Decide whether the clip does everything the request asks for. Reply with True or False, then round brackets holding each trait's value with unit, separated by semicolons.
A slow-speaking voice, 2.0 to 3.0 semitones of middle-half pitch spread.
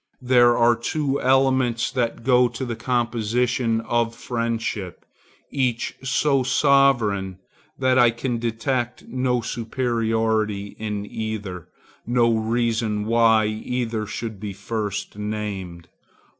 True (110 wpm; 2.4 semitones)